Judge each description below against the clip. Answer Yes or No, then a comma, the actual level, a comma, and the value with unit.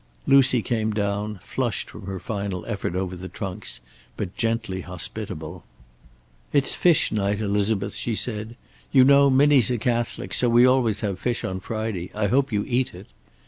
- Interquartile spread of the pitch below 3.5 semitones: No, average, 3.8 semitones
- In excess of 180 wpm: No, average, 165 wpm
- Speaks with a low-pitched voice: Yes, low, 110 Hz